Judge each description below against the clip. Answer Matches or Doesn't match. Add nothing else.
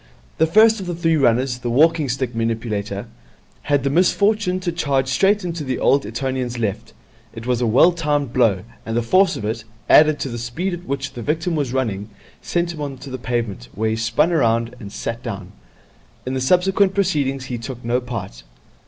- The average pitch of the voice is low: Matches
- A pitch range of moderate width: Doesn't match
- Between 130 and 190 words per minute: Doesn't match